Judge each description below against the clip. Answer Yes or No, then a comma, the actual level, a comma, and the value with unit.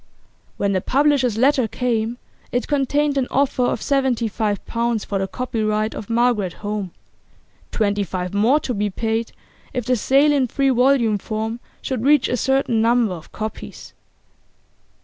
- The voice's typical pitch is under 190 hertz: No, high, 235 Hz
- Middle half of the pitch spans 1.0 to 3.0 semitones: No, average, 3.7 semitones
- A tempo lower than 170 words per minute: Yes, average, 155 wpm